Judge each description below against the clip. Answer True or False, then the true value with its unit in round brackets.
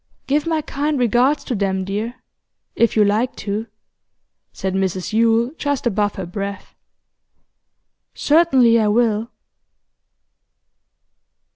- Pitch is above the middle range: True (230 Hz)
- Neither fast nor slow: False (110 wpm)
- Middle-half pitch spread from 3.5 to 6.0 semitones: True (4.3 semitones)